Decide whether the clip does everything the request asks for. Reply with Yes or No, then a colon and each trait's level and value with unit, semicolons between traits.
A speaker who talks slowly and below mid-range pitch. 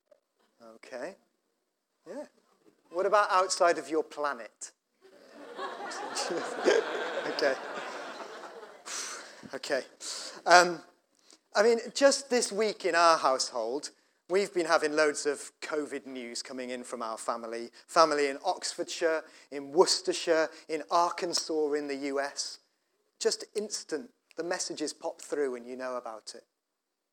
No: slow, 115 wpm; medium, 165 Hz